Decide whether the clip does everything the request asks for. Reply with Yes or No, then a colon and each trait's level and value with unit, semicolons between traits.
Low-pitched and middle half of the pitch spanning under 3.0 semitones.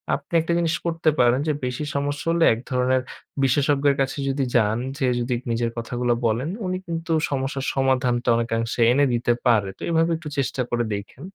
No: low, 130 Hz; average, 3.3 semitones